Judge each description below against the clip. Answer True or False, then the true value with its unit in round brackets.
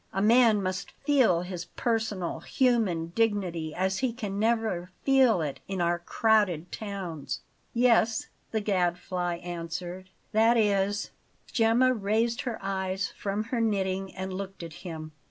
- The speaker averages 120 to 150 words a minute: True (140 wpm)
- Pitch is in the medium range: False (195 Hz)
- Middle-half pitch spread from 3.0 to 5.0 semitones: True (4.0 semitones)